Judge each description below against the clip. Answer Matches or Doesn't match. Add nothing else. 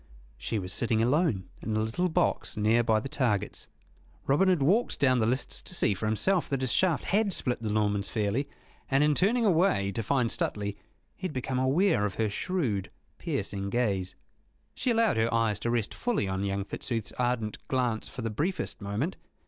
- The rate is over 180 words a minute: Matches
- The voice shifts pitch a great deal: Matches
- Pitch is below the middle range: Matches